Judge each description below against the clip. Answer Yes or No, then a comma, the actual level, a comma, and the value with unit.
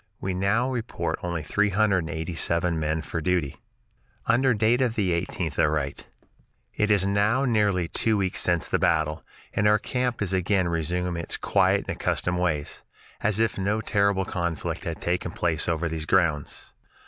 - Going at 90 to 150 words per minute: No, average, 175 wpm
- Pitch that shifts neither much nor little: Yes, average, 4.0 semitones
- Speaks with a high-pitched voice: No, very low, 90 Hz